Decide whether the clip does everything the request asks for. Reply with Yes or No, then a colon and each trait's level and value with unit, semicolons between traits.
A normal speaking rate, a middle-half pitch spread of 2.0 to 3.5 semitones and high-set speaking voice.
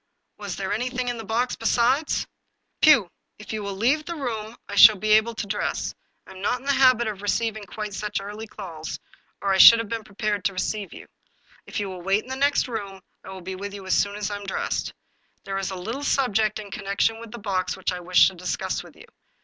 No: fast, 240 wpm; average, 3.0 semitones; high, 210 Hz